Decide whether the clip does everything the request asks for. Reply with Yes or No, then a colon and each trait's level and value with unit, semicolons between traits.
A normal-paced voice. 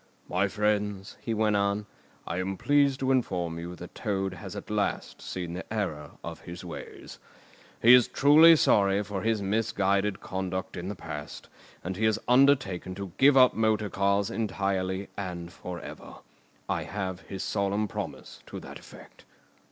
Yes: average, 165 wpm